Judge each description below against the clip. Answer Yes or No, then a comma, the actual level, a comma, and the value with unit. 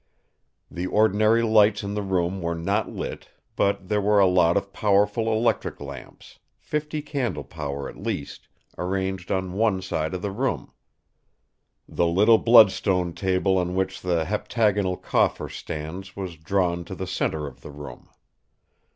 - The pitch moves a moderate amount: Yes, average, 3.0 semitones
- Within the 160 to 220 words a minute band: No, average, 150 wpm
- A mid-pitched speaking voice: No, very low, 95 Hz